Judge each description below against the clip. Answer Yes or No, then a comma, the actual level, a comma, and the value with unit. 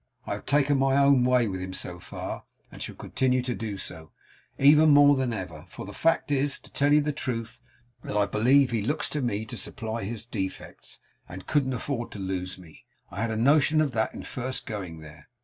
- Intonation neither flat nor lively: No, wide, 5.8 semitones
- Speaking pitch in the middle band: No, low, 120 Hz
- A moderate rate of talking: No, fast, 220 wpm